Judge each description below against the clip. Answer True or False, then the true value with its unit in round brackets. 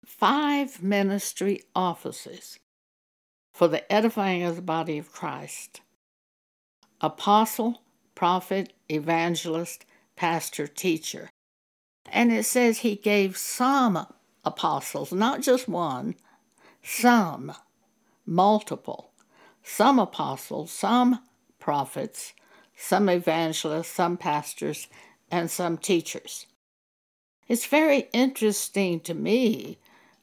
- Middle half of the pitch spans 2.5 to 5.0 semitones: False (5.6 semitones)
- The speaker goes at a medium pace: False (85 wpm)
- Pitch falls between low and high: False (195 Hz)